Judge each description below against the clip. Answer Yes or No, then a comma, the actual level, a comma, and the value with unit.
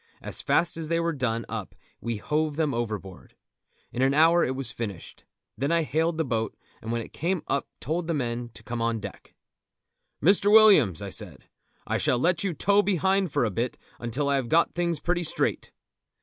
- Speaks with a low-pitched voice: No, medium, 145 Hz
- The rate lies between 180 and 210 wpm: Yes, average, 200 wpm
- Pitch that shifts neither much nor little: No, wide, 6.2 semitones